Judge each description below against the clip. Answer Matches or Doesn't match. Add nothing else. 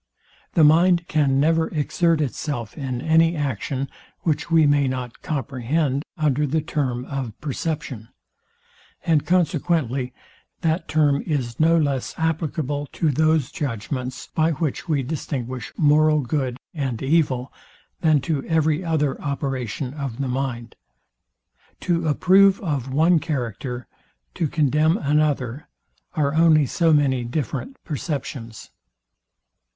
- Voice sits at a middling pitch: Matches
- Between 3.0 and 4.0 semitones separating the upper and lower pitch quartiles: Matches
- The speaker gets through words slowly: Matches